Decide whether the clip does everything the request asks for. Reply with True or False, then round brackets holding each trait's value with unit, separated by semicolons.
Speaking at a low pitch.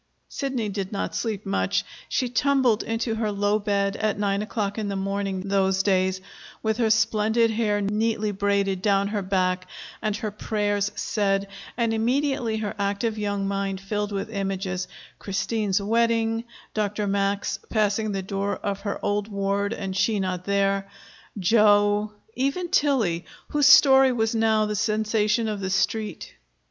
False (205 Hz)